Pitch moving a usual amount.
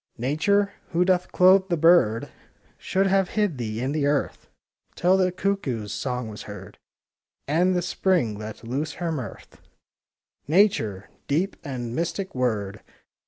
No: wide, 7.9 semitones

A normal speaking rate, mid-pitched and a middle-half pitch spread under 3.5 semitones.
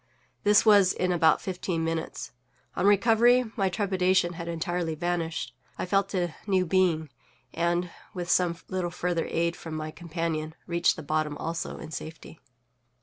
Yes: average, 150 wpm; medium, 175 Hz; narrow, 2.4 semitones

